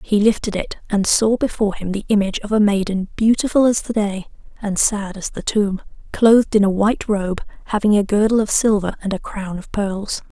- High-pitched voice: Yes, high, 205 Hz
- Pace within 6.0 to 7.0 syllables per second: No, 5.4 syllables/s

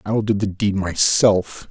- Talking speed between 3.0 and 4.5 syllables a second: Yes, 3.7 syllables/s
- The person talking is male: Yes, male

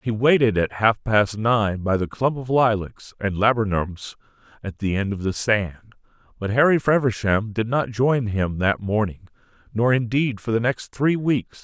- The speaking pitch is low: Yes, low, 110 Hz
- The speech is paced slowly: No, average, 180 wpm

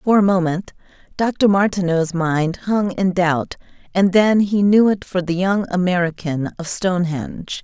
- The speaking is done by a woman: Yes, female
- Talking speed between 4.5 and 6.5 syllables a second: No, 4.3 syllables/s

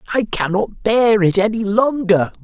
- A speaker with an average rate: Yes, average, 150 wpm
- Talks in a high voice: Yes, high, 210 Hz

